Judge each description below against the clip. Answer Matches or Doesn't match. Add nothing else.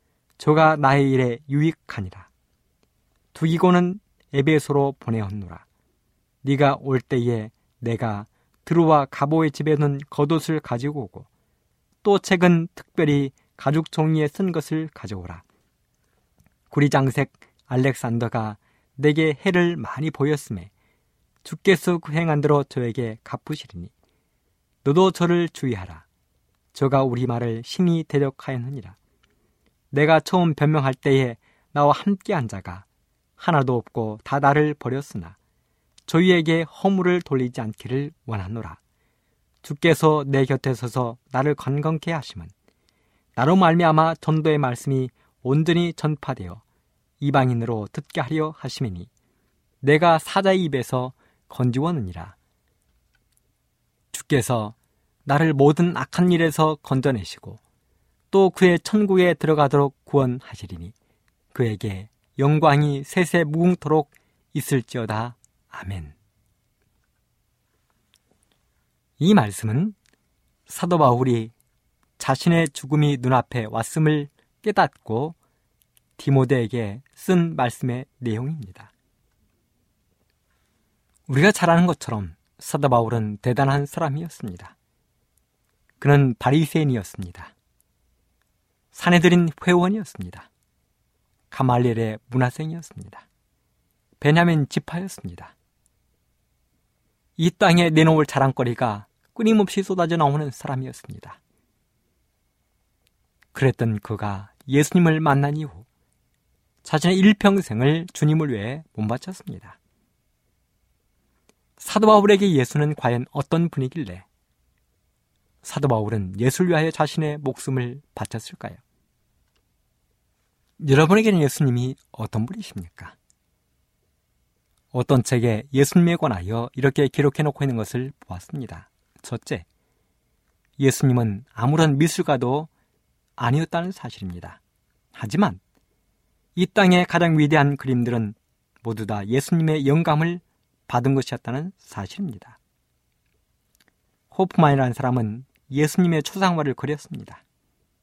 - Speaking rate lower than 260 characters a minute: Matches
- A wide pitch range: Matches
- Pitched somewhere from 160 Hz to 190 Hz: Doesn't match